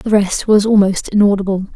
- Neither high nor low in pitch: No, high, 200 Hz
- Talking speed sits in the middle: Yes, average, 170 wpm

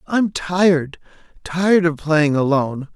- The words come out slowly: Yes, slow, 100 wpm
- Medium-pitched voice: Yes, medium, 165 Hz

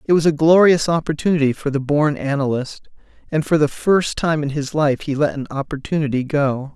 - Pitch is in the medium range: Yes, medium, 150 Hz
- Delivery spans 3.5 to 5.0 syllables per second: No, 5.4 syllables/s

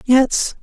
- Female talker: Yes, female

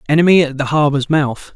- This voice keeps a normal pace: Yes, average, 195 wpm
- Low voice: No, medium, 145 Hz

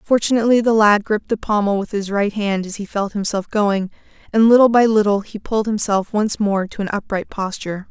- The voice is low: No, high, 210 Hz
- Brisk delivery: Yes, fast, 215 wpm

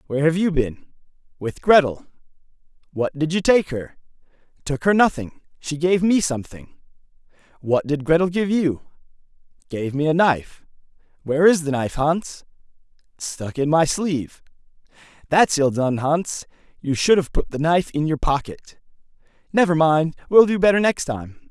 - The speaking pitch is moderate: Yes, medium, 155 Hz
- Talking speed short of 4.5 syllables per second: No, 4.9 syllables/s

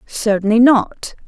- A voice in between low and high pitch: No, high, 225 Hz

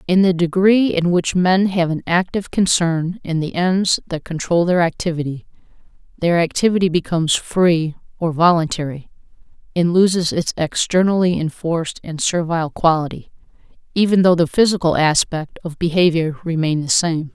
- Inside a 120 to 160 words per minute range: Yes, average, 140 wpm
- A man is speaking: No, female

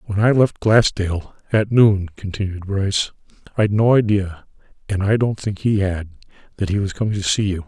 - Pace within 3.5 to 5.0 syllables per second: No, 5.2 syllables/s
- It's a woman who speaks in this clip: No, male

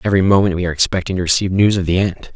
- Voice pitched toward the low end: Yes, very low, 95 Hz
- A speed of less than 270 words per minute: No, fast, 280 wpm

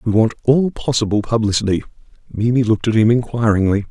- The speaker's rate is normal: Yes, average, 155 wpm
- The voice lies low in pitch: Yes, low, 110 Hz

